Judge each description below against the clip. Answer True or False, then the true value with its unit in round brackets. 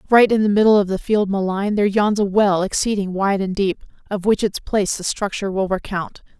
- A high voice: True (200 Hz)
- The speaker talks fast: True (225 wpm)